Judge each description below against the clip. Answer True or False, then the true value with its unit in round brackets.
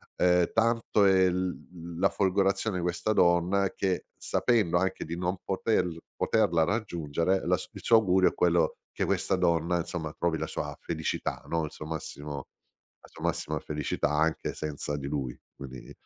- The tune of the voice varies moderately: True (3.2 semitones)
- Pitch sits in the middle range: False (85 Hz)